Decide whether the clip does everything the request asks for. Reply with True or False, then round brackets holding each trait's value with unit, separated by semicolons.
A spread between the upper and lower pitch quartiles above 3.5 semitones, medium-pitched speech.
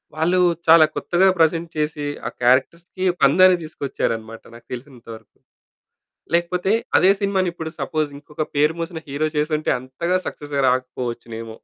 True (4.9 semitones; 155 Hz)